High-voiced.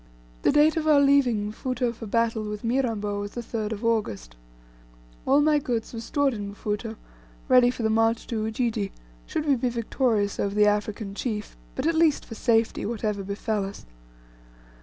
Yes: high, 225 Hz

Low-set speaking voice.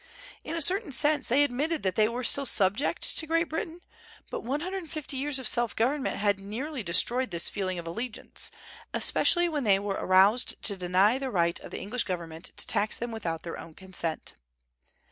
No: high, 235 Hz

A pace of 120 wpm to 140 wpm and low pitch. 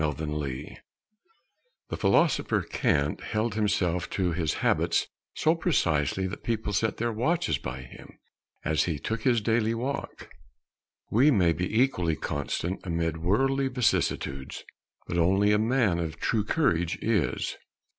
Yes: slow, 135 wpm; very low, 95 Hz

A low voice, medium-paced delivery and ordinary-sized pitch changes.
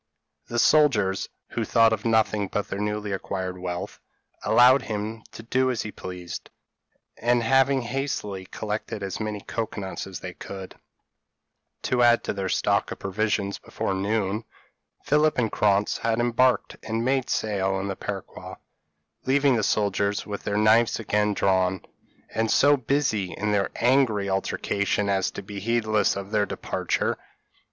Yes: low, 105 Hz; average, 155 wpm; average, 3.2 semitones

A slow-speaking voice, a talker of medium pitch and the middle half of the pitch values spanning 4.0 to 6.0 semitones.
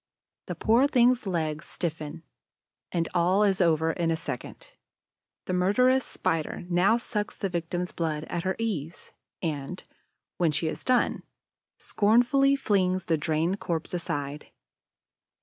Yes: slow, 130 wpm; medium, 175 Hz; average, 4.4 semitones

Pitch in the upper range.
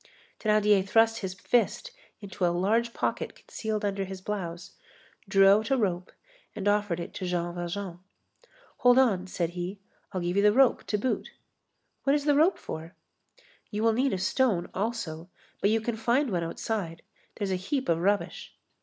Yes: high, 200 Hz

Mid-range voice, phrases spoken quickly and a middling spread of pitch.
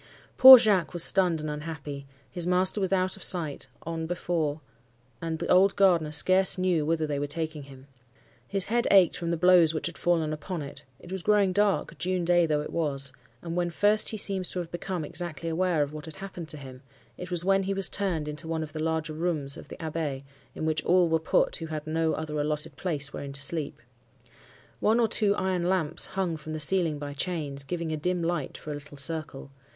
Yes: medium, 165 Hz; fast, 215 wpm; average, 3.3 semitones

